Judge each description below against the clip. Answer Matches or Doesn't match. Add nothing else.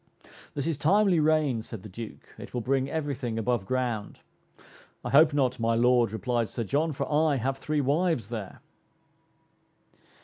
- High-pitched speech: Doesn't match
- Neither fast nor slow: Matches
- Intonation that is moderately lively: Matches